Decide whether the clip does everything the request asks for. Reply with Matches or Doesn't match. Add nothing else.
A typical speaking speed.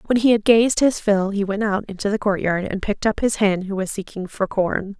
Doesn't match